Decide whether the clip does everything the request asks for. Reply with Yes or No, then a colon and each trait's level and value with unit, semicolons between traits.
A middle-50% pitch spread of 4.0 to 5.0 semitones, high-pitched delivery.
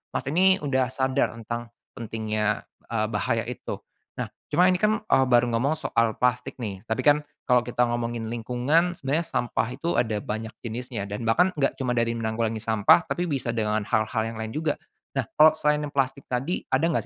No: average, 4.4 semitones; low, 120 Hz